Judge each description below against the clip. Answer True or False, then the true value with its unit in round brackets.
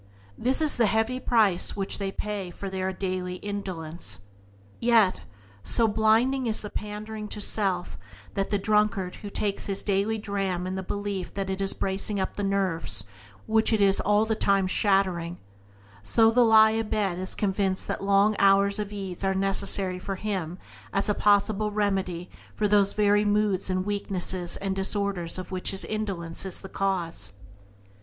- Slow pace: False (180 wpm)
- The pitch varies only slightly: True (1.9 semitones)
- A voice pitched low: False (200 Hz)